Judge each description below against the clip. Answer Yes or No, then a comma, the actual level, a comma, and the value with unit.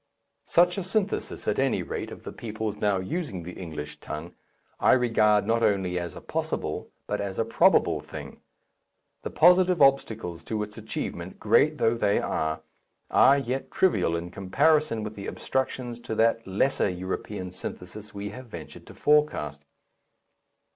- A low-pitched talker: Yes, low, 105 Hz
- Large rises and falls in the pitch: Yes, wide, 6.2 semitones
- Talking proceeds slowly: No, average, 155 wpm